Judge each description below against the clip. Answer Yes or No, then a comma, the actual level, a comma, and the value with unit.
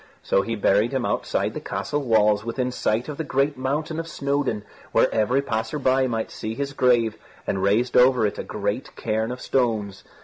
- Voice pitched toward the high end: No, low, 125 Hz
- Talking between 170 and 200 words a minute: Yes, average, 195 wpm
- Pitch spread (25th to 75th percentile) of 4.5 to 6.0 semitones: No, average, 3.9 semitones